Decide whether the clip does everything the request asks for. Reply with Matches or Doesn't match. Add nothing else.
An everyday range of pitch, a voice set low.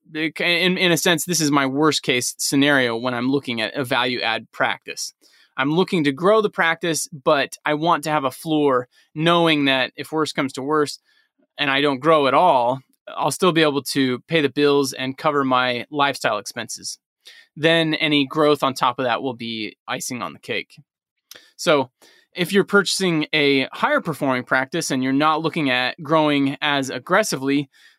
Doesn't match